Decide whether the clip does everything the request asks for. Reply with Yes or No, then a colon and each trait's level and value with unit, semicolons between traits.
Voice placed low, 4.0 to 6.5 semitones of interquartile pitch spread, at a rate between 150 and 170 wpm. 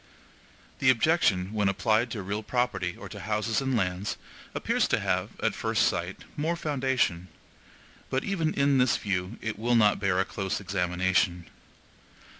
Yes: low, 105 Hz; wide, 5.5 semitones; average, 155 wpm